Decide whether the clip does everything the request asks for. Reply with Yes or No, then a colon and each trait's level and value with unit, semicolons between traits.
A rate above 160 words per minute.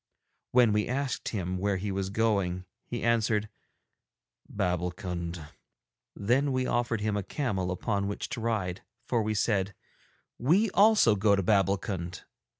No: average, 140 wpm